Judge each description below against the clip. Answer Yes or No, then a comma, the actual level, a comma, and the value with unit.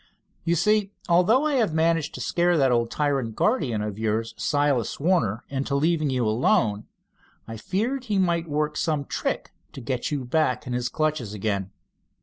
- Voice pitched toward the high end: No, medium, 145 Hz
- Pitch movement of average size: No, wide, 6.4 semitones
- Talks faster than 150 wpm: Yes, average, 170 wpm